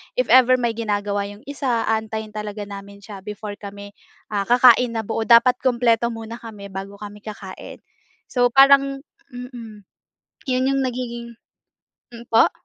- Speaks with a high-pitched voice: Yes, high, 225 Hz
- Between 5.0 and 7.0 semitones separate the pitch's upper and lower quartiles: No, average, 3.2 semitones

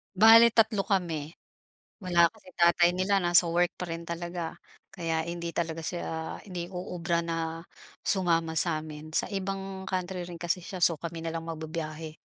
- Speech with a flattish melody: Yes, narrow, 2.1 semitones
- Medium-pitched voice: Yes, medium, 170 Hz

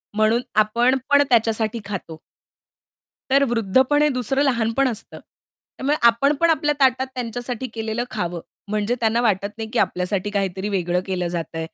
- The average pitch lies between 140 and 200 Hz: No, high, 225 Hz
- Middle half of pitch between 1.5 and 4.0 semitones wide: No, average, 4.4 semitones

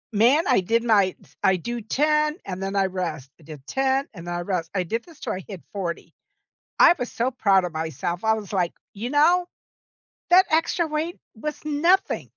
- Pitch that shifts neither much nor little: No, wide, 8.4 semitones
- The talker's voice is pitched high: Yes, high, 220 Hz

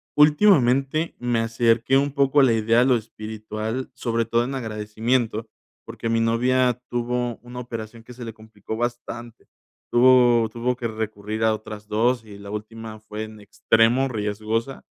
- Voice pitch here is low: Yes, low, 115 Hz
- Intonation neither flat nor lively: No, narrow, 2.2 semitones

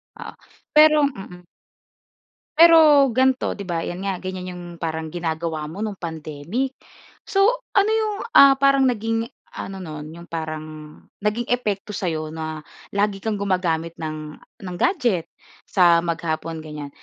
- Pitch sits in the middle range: Yes, medium, 180 Hz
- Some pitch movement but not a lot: No, wide, 6.3 semitones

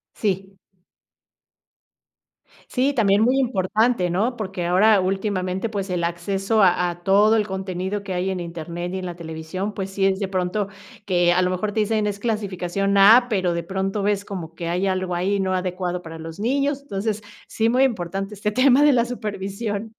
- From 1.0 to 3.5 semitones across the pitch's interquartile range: Yes, average, 2.8 semitones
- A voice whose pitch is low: No, high, 195 Hz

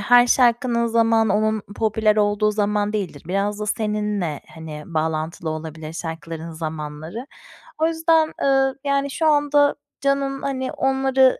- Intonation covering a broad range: Yes, wide, 8.1 semitones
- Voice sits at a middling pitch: No, high, 215 Hz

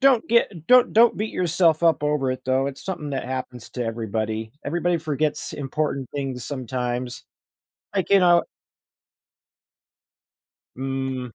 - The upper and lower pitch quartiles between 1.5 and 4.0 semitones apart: No, average, 5.1 semitones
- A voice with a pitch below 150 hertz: Yes, medium, 140 Hz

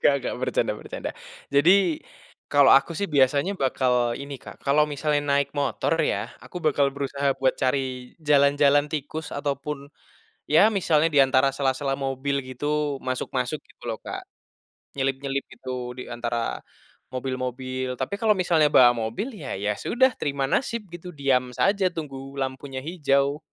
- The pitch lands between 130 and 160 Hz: Yes, medium, 140 Hz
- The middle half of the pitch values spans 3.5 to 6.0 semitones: No, narrow, 2.4 semitones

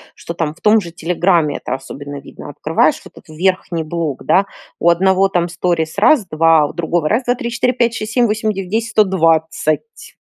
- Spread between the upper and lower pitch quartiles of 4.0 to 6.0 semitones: Yes, average, 4.9 semitones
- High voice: No, medium, 175 Hz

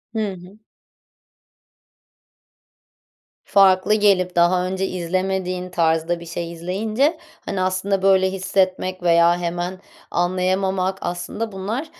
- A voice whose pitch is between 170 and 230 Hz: Yes, medium, 185 Hz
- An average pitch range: No, narrow, 1.6 semitones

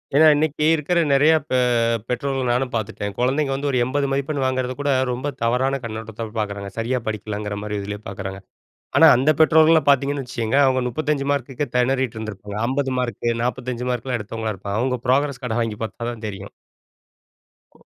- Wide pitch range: No, average, 3.9 semitones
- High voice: No, low, 125 Hz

